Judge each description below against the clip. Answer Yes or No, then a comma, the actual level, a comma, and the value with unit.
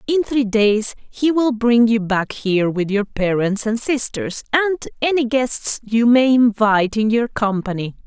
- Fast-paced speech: No, average, 170 wpm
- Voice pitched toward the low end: No, high, 230 Hz